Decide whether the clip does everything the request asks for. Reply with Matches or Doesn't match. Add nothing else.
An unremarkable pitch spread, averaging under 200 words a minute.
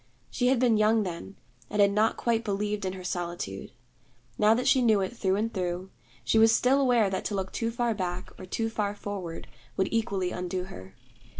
Doesn't match